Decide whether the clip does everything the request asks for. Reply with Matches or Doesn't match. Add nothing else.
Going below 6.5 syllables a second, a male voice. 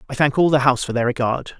Doesn't match